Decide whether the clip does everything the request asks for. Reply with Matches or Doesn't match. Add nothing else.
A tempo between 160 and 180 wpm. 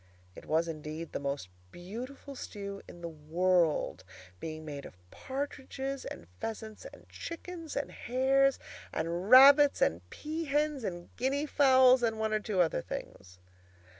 Doesn't match